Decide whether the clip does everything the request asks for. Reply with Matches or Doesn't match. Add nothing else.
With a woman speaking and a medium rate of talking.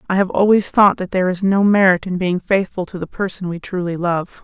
Doesn't match